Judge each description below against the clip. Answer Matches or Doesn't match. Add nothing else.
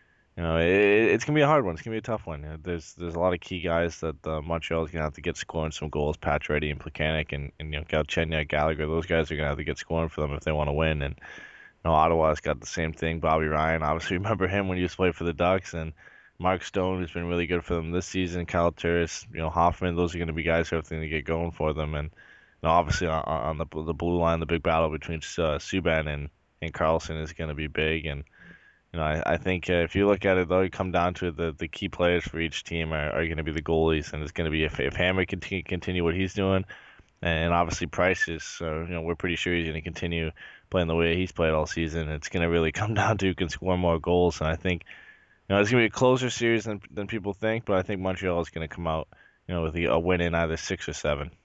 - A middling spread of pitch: Doesn't match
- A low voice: Matches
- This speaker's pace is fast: Matches